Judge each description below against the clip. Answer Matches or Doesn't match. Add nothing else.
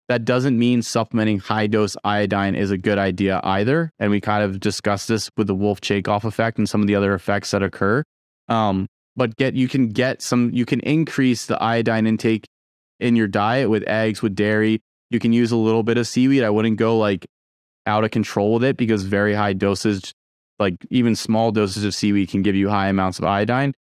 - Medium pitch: Doesn't match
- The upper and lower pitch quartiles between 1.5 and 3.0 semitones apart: Matches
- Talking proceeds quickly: Matches